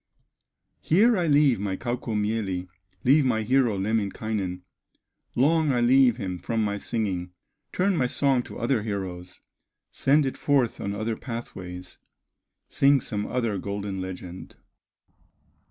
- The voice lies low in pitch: Yes, low, 110 Hz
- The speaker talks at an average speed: No, slow, 125 wpm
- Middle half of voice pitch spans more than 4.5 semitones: Yes, average, 5.2 semitones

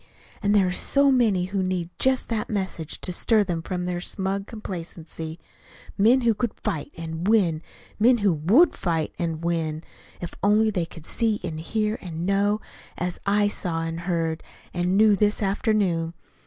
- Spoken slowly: No, average, 170 wpm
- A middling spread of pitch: Yes, average, 4.1 semitones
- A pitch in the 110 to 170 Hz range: No, medium, 185 Hz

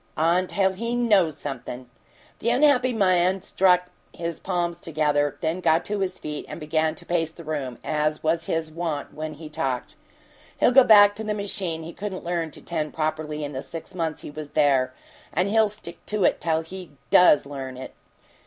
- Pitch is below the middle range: No, medium, 165 Hz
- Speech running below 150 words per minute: No, average, 190 wpm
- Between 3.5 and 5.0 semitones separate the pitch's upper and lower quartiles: Yes, average, 3.8 semitones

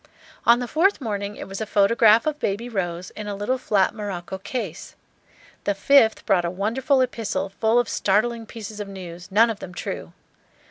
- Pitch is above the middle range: Yes, high, 210 Hz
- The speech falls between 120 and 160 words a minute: No, average, 185 wpm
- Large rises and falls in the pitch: No, average, 3.2 semitones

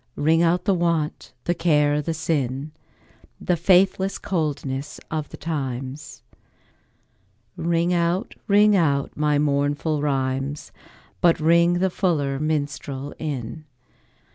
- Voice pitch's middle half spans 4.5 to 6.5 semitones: No, average, 3.2 semitones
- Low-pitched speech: No, medium, 155 Hz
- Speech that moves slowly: Yes, slow, 115 wpm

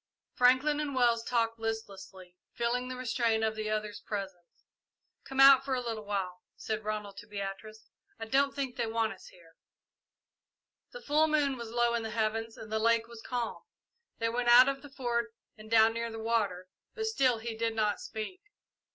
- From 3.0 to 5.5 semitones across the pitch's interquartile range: No, narrow, 2.5 semitones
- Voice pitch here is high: Yes, high, 230 Hz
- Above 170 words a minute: Yes, average, 185 wpm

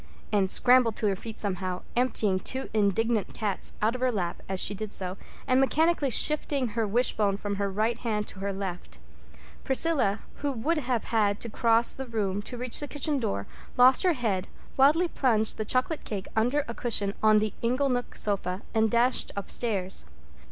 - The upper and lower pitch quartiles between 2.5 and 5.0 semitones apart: Yes, average, 4.1 semitones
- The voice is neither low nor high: No, high, 225 Hz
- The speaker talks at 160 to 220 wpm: Yes, average, 180 wpm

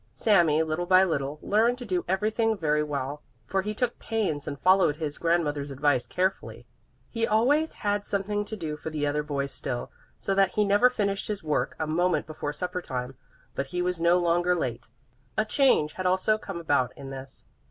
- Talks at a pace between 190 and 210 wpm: Yes, average, 195 wpm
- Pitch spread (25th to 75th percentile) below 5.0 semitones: No, wide, 5.5 semitones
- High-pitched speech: No, medium, 175 Hz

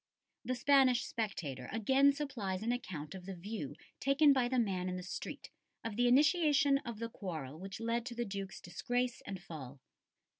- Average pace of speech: Yes, average, 180 wpm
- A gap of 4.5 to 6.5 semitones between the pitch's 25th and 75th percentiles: Yes, wide, 5.5 semitones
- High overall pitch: Yes, high, 225 Hz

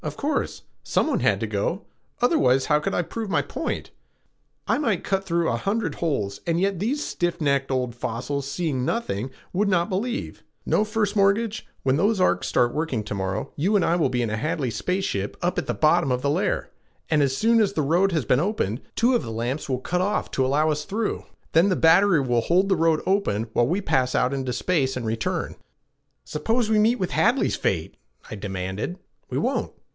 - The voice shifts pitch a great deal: Yes, wide, 7.7 semitones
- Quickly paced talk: Yes, fast, 210 wpm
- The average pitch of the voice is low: No, medium, 160 Hz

